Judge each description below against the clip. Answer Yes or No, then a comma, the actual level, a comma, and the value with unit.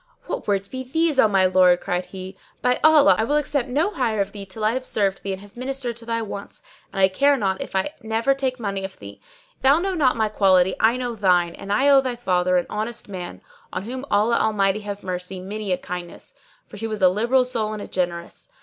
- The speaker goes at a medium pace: No, fast, 240 wpm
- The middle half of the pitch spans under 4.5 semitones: No, average, 4.9 semitones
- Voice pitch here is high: Yes, high, 215 Hz